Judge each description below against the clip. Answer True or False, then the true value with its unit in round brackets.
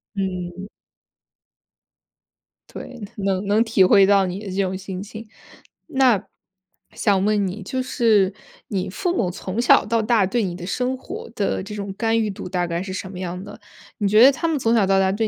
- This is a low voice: False (200 Hz)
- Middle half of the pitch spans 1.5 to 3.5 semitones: True (3.1 semitones)